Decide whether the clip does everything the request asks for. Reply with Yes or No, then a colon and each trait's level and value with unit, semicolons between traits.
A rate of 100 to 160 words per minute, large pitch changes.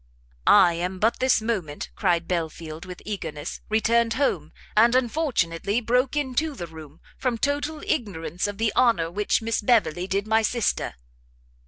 Yes: average, 150 wpm; wide, 5.9 semitones